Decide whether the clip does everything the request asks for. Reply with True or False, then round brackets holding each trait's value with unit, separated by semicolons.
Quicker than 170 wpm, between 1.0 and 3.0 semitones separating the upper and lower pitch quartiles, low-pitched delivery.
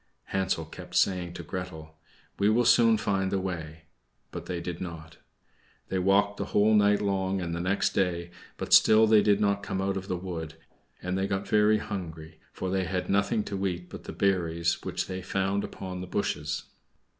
True (190 wpm; 2.4 semitones; 95 Hz)